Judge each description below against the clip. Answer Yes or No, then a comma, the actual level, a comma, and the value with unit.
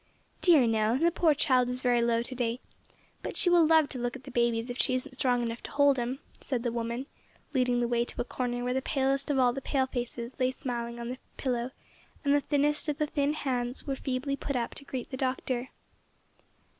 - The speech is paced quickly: Yes, fast, 230 wpm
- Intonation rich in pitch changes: No, narrow, 2.4 semitones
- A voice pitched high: Yes, very high, 255 Hz